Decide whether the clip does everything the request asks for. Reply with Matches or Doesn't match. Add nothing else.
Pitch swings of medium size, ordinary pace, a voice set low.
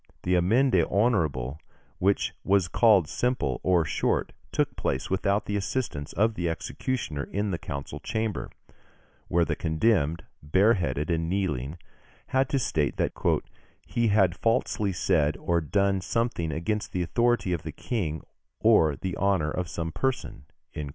Matches